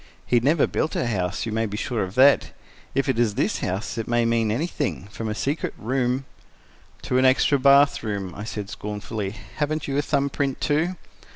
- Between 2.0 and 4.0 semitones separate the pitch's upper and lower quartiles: No, average, 4.7 semitones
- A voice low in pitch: Yes, low, 120 Hz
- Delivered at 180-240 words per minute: Yes, average, 200 wpm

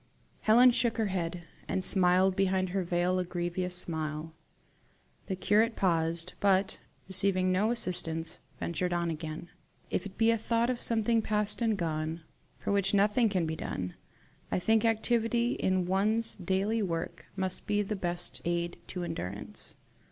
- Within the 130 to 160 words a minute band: Yes, average, 155 wpm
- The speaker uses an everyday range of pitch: Yes, average, 3.7 semitones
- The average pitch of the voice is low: No, medium, 185 Hz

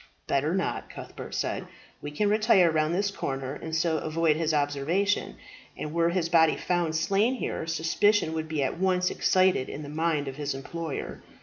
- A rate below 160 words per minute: No, average, 180 wpm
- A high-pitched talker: No, medium, 160 Hz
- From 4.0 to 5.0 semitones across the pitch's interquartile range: No, average, 3.2 semitones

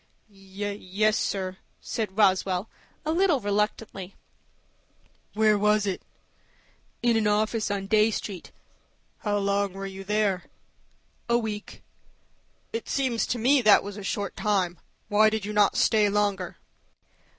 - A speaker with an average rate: No, slow, 130 wpm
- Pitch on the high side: Yes, high, 205 Hz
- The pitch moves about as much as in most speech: No, narrow, 1.8 semitones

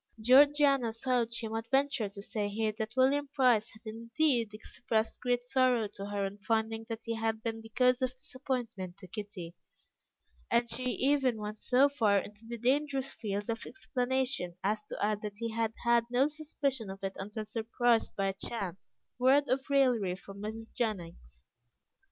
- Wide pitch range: No, average, 3.5 semitones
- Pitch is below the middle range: No, high, 230 Hz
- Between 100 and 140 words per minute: No, average, 175 wpm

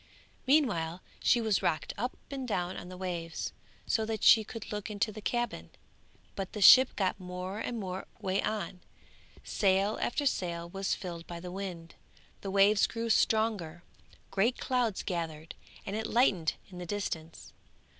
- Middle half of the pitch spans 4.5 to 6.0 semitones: No, average, 3.7 semitones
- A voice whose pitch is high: Yes, high, 195 Hz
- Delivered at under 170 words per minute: Yes, average, 160 wpm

